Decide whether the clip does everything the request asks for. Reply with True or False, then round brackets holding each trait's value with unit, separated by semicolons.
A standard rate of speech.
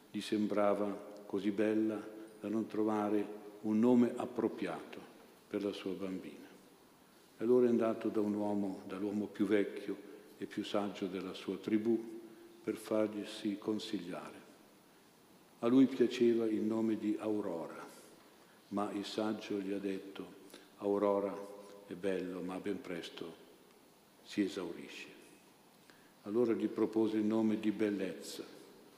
True (125 wpm)